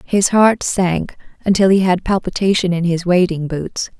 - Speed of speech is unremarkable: Yes, average, 165 wpm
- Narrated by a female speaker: Yes, female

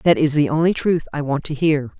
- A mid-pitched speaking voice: Yes, medium, 150 Hz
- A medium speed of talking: No, fast, 270 wpm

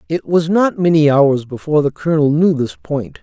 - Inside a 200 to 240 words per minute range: Yes, fast, 205 wpm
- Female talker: No, male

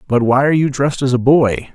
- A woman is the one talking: No, male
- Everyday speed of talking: No, fast, 275 wpm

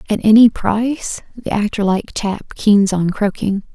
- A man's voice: No, female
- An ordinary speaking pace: Yes, average, 160 wpm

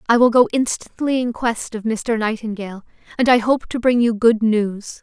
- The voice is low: No, high, 230 Hz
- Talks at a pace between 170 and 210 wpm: Yes, fast, 205 wpm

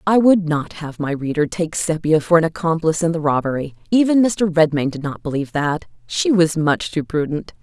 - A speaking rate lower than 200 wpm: No, fast, 205 wpm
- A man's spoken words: No, female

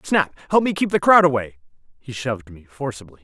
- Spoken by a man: Yes, male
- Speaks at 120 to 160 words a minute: No, fast, 205 wpm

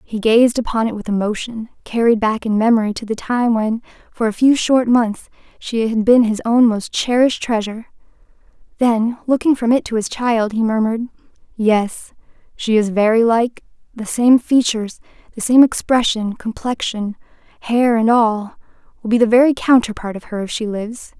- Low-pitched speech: No, high, 225 Hz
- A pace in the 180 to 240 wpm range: No, average, 165 wpm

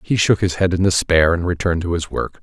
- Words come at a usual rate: No, fast, 270 wpm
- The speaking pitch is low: Yes, very low, 85 Hz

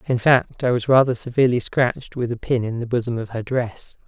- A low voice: Yes, low, 120 Hz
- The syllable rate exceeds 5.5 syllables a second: Yes, 5.7 syllables/s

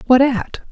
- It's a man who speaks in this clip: No, female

